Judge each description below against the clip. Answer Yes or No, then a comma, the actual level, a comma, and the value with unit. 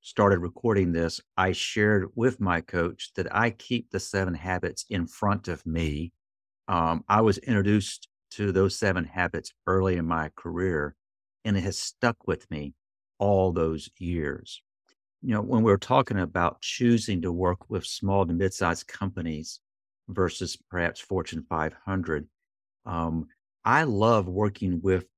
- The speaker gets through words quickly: No, average, 150 wpm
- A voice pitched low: Yes, very low, 95 Hz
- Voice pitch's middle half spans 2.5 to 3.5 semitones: Yes, average, 3.2 semitones